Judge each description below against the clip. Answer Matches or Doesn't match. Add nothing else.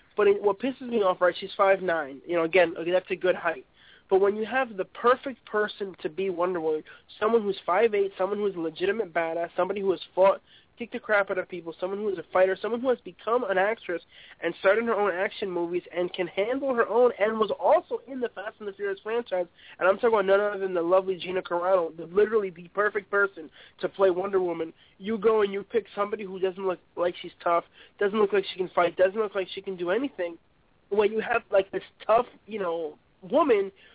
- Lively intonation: Doesn't match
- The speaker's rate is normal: Doesn't match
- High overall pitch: Matches